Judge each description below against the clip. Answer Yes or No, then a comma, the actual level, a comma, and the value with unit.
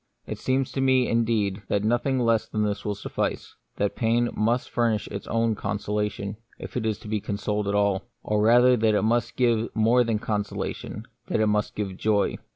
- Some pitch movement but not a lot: No, narrow, 2.2 semitones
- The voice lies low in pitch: Yes, low, 110 Hz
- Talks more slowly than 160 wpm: No, average, 200 wpm